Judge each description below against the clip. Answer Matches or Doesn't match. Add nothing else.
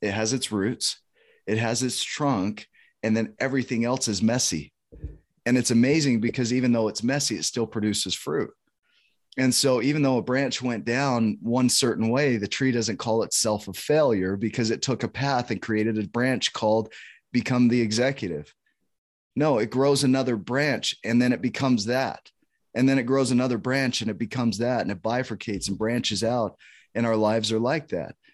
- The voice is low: Matches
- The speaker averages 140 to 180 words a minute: Doesn't match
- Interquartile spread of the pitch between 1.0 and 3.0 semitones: Matches